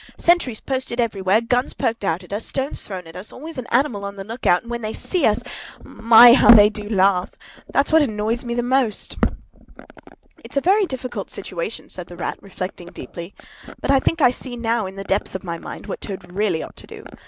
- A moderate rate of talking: No, fast, 215 wpm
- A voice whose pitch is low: No, high, 220 Hz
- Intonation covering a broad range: No, average, 4.6 semitones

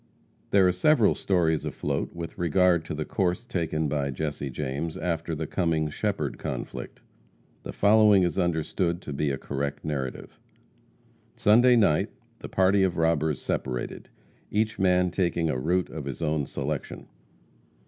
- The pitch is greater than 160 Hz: No, very low, 80 Hz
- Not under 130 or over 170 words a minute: Yes, average, 150 wpm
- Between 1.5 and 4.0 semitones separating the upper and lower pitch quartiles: Yes, average, 3.7 semitones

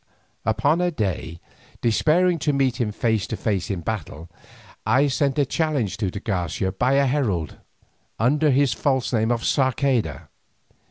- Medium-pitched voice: No, low, 120 Hz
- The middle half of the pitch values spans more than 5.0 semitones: Yes, wide, 5.6 semitones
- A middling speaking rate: Yes, average, 155 wpm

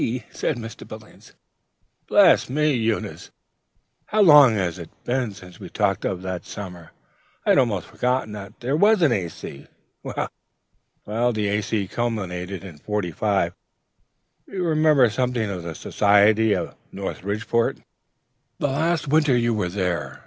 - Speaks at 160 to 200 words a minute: No, average, 140 wpm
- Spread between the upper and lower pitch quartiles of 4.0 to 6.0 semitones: Yes, average, 5.2 semitones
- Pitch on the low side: Yes, low, 110 Hz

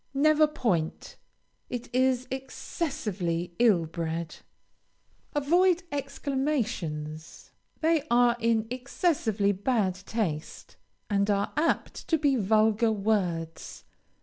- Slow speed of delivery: Yes, slow, 95 wpm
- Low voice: No, high, 225 Hz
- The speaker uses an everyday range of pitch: No, wide, 6.8 semitones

